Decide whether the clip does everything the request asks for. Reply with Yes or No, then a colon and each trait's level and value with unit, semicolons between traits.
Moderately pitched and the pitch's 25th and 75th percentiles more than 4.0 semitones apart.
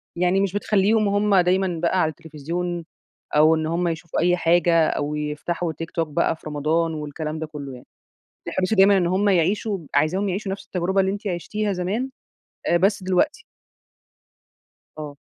No: medium, 175 Hz; average, 3.4 semitones